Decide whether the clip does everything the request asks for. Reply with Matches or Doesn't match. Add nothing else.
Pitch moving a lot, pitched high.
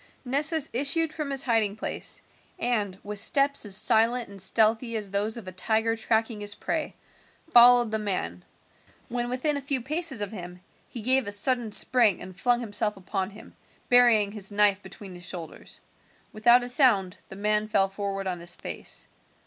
Doesn't match